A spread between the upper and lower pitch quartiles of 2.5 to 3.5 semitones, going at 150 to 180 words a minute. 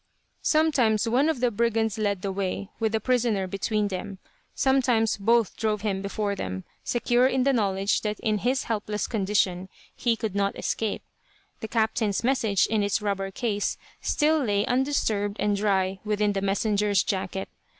Yes: average, 2.8 semitones; average, 160 wpm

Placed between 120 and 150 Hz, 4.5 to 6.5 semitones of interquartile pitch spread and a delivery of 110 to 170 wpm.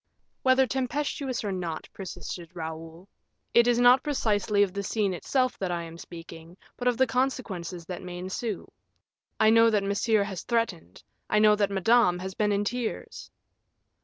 No: high, 205 Hz; average, 4.9 semitones; average, 165 wpm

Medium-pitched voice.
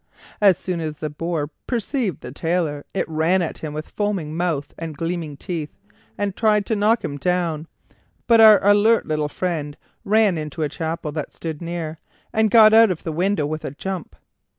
Yes: medium, 170 Hz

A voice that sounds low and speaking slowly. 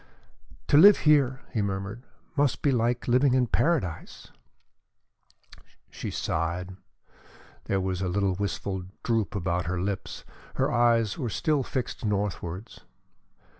Yes: low, 105 Hz; slow, 125 wpm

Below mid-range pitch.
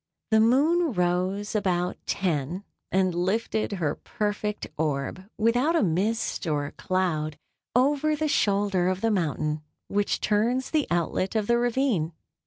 No: high, 200 Hz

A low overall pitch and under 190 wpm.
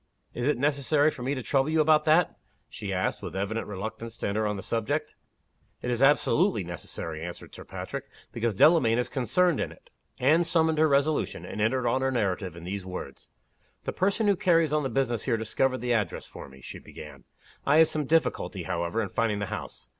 No: low, 125 Hz; fast, 205 wpm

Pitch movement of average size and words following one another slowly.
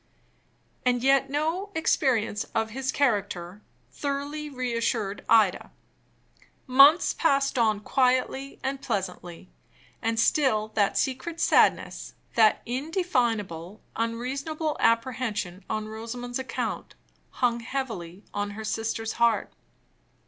Yes: average, 4.1 semitones; slow, 105 wpm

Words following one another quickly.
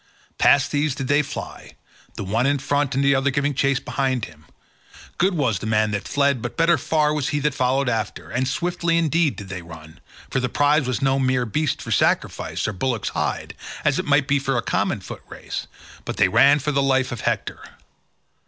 Yes: fast, 210 wpm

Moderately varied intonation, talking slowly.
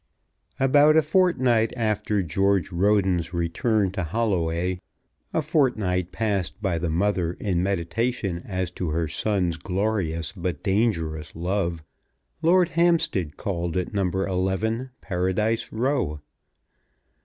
Yes: average, 4.4 semitones; slow, 115 wpm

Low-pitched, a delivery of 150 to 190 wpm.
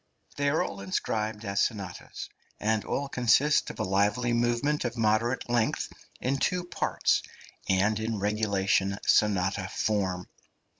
No: low, 110 Hz; slow, 135 wpm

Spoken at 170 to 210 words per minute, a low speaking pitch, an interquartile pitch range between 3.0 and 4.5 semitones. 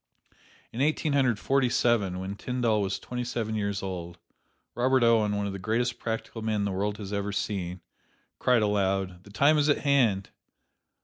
Yes: average, 175 wpm; low, 105 Hz; average, 3.8 semitones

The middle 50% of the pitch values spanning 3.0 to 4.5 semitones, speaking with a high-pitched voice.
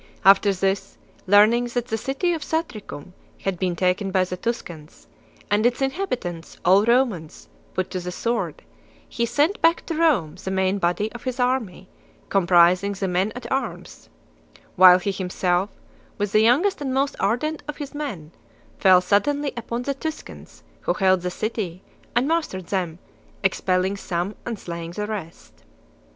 No: wide, 5.4 semitones; high, 200 Hz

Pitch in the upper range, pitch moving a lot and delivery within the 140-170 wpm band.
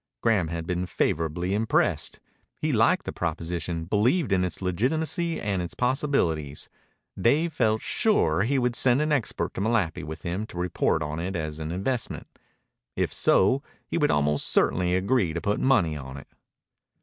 No: very low, 95 Hz; wide, 6.9 semitones; average, 165 wpm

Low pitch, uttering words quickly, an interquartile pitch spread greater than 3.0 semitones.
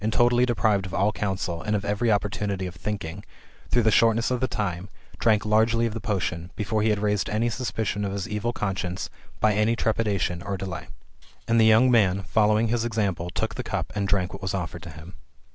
No: low, 105 Hz; fast, 210 wpm; average, 2.7 semitones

